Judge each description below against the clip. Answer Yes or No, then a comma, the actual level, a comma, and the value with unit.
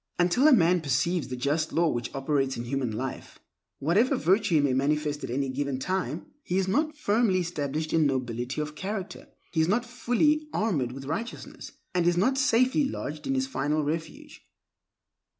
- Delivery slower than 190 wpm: Yes, average, 180 wpm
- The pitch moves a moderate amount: No, wide, 7.0 semitones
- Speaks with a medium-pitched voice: Yes, medium, 160 Hz